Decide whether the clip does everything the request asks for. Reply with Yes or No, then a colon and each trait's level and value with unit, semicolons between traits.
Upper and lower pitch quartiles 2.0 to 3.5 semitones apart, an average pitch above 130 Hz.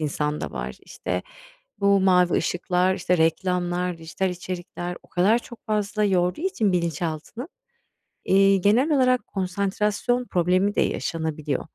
Yes: average, 2.8 semitones; medium, 185 Hz